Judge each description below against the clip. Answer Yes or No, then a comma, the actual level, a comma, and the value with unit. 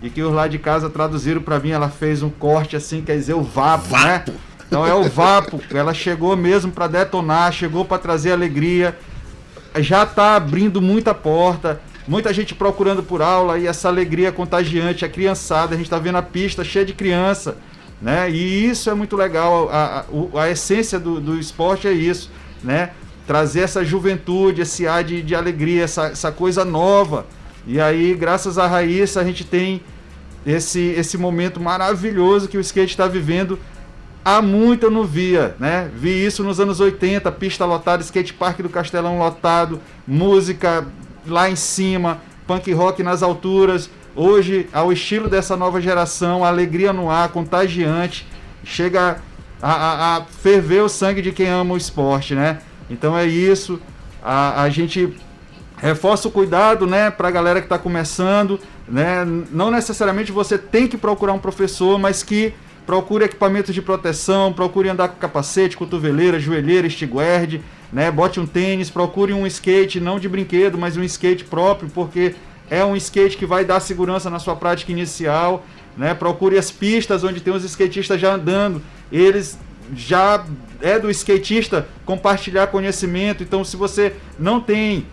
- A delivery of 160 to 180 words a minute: Yes, average, 165 wpm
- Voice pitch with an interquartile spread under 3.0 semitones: Yes, narrow, 2.5 semitones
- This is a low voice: No, medium, 180 Hz